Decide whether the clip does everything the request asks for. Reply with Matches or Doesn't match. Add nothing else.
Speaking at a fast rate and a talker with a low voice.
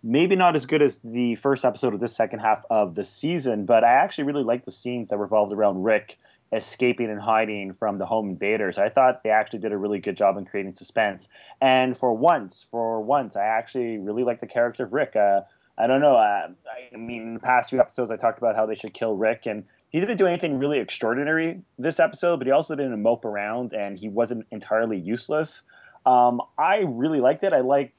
Matches